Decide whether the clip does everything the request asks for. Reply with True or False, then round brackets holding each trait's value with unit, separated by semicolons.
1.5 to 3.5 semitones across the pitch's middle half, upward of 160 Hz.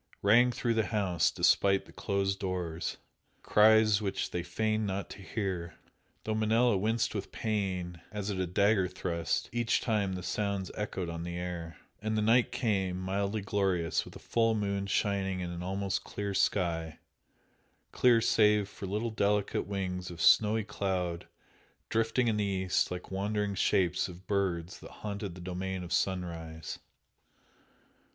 False (2.7 semitones; 100 Hz)